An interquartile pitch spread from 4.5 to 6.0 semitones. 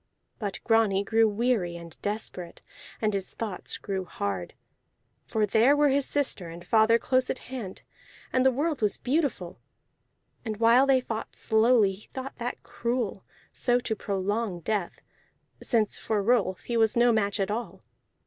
No: average, 3.8 semitones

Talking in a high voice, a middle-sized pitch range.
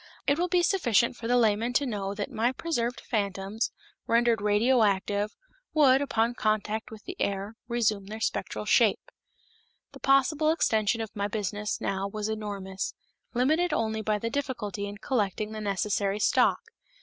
Yes: high, 220 Hz; average, 3.2 semitones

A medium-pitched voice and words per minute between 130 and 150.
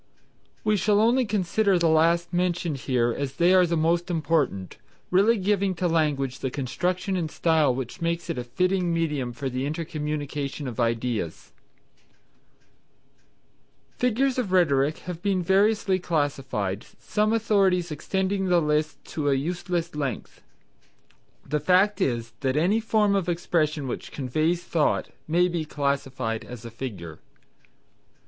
Yes: medium, 165 Hz; average, 140 wpm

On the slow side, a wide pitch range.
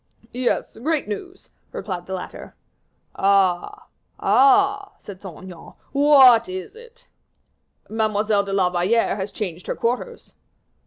Yes: slow, 120 wpm; wide, 6.6 semitones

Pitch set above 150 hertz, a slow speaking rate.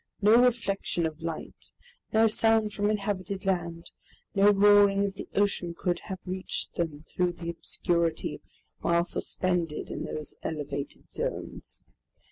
Yes: medium, 185 Hz; slow, 130 wpm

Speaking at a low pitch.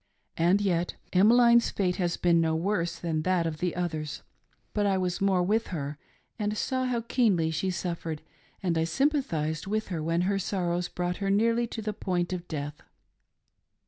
No: medium, 180 Hz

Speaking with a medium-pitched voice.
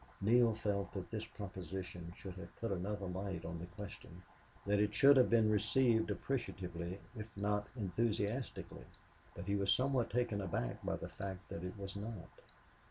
No: low, 100 Hz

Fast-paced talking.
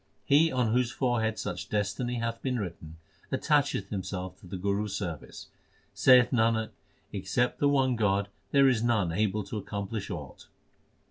No: average, 155 wpm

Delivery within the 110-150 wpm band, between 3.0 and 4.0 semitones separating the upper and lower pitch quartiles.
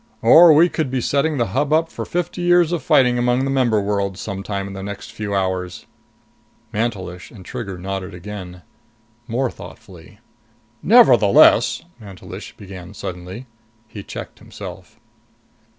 No: average, 145 wpm; wide, 5.6 semitones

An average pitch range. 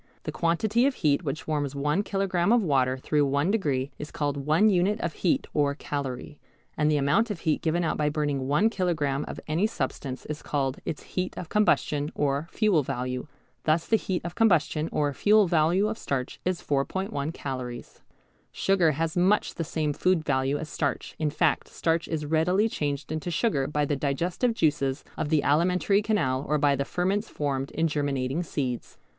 Yes: average, 4.2 semitones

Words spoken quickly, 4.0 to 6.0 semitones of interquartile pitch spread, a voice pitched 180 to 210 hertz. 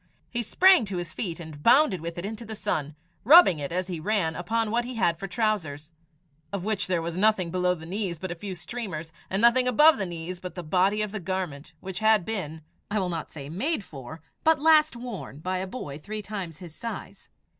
Yes: fast, 220 wpm; average, 4.7 semitones; medium, 185 Hz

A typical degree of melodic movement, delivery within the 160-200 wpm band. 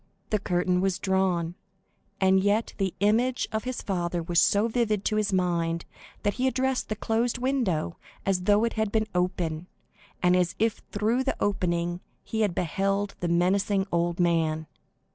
Yes: average, 3.7 semitones; average, 165 wpm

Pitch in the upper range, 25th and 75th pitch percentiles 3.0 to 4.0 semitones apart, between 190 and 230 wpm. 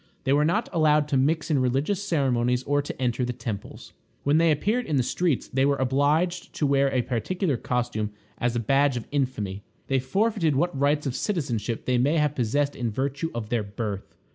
No: low, 135 Hz; average, 3.7 semitones; average, 200 wpm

